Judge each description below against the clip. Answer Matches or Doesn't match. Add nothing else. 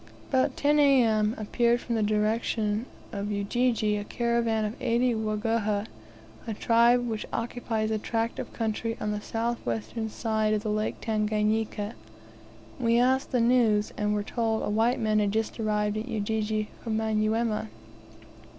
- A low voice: Doesn't match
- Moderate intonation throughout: Doesn't match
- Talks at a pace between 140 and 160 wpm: Matches